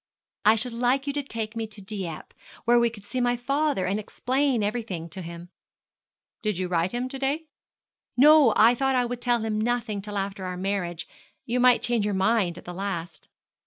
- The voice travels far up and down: No, average, 4.2 semitones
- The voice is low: No, high, 225 Hz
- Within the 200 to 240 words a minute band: Yes, fast, 205 wpm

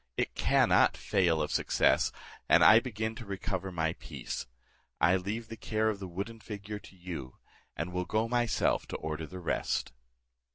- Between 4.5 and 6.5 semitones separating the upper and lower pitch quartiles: No, average, 3.9 semitones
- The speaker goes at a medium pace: Yes, average, 170 wpm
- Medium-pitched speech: No, very low, 95 Hz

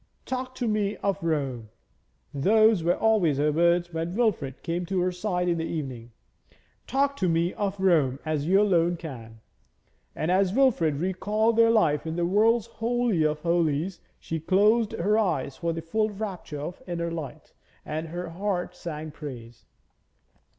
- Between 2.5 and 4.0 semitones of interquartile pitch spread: No, average, 4.9 semitones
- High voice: No, medium, 175 Hz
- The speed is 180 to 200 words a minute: No, average, 165 wpm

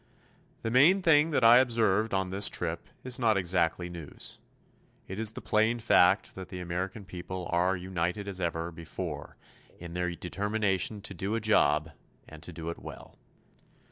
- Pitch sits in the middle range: No, very low, 95 Hz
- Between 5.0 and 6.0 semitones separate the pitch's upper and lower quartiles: No, average, 4.0 semitones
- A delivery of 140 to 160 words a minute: No, average, 170 wpm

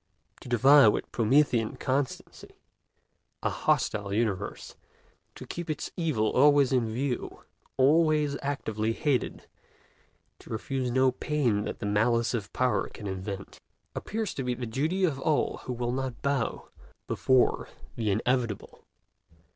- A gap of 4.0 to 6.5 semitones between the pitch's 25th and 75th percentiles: Yes, average, 4.3 semitones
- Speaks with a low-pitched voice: Yes, low, 125 Hz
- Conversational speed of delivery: No, slow, 130 wpm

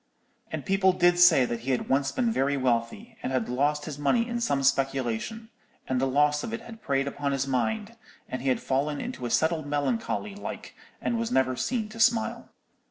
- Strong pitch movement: Yes, wide, 8.6 semitones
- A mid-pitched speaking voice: Yes, medium, 145 Hz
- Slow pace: No, fast, 205 wpm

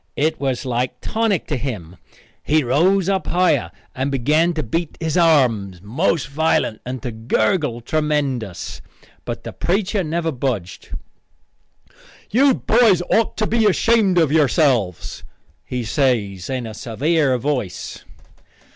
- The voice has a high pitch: No, medium, 145 Hz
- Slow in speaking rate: Yes, slow, 130 wpm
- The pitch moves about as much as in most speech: No, wide, 6.1 semitones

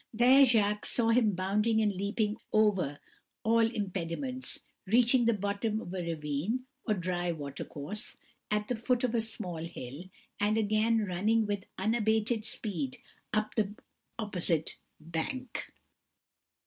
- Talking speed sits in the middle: No, slow, 130 wpm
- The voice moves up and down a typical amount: Yes, average, 3.9 semitones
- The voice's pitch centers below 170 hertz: No, high, 210 Hz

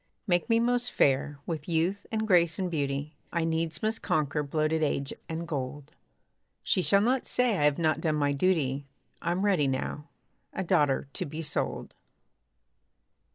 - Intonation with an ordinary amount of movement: Yes, average, 4.3 semitones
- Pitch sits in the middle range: Yes, medium, 160 Hz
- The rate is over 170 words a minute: No, average, 160 wpm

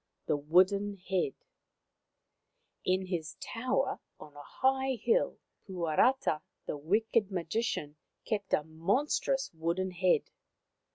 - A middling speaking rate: No, slow, 105 wpm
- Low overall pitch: No, medium, 185 Hz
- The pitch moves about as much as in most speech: No, wide, 5.9 semitones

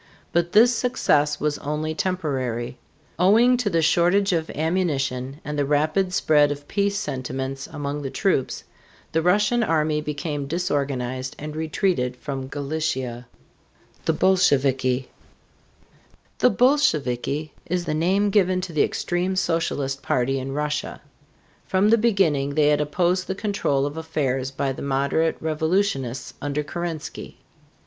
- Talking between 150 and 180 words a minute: No, average, 140 wpm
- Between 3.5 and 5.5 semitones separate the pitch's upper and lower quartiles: Yes, average, 4.7 semitones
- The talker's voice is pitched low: No, medium, 150 Hz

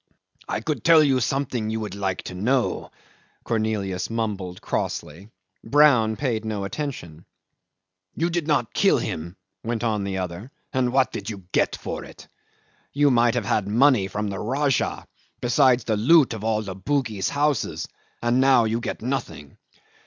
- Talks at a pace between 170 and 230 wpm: No, average, 160 wpm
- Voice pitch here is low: Yes, low, 115 Hz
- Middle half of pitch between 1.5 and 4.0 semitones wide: No, average, 5.0 semitones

